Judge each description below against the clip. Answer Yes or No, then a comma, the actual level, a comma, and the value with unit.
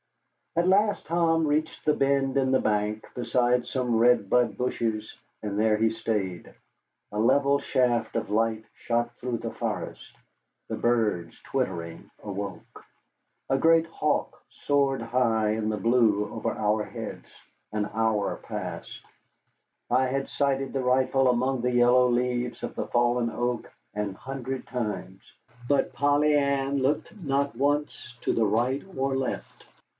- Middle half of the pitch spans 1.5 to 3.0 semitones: No, average, 3.6 semitones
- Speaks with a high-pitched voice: No, low, 125 Hz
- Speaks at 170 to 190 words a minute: No, average, 145 wpm